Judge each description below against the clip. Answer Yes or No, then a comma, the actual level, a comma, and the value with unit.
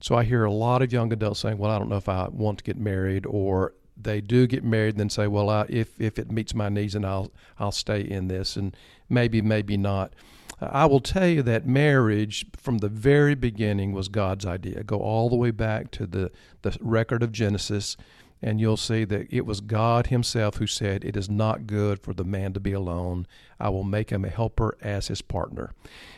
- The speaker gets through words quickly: Yes, fast, 225 wpm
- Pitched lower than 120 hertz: Yes, low, 105 Hz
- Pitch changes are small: Yes, narrow, 2.3 semitones